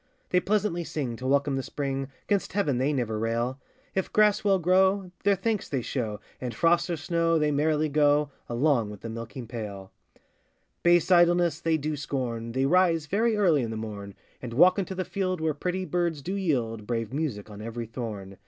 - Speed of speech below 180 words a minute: No, average, 190 wpm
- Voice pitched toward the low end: No, medium, 145 Hz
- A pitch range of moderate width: No, wide, 7.2 semitones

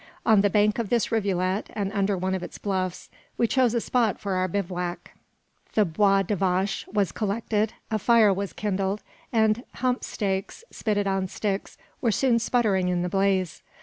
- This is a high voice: Yes, high, 200 Hz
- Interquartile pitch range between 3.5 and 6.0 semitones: No, narrow, 2.5 semitones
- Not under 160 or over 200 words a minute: Yes, average, 180 wpm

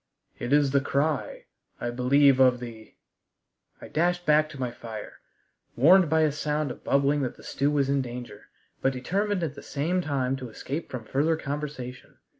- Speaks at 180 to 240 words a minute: Yes, average, 185 wpm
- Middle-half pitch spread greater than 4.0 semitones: No, average, 3.2 semitones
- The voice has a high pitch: No, medium, 140 Hz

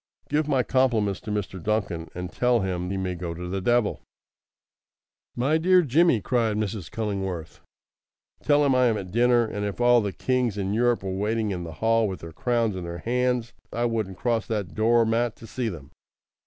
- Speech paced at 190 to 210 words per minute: Yes, average, 195 wpm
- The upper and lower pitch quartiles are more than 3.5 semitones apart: Yes, average, 4.2 semitones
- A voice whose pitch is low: Yes, low, 110 Hz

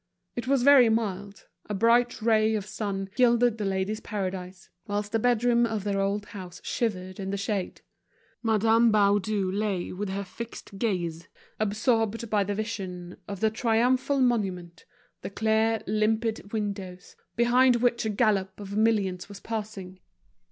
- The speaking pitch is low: No, high, 210 Hz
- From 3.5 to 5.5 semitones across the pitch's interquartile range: No, average, 2.7 semitones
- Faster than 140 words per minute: Yes, average, 150 wpm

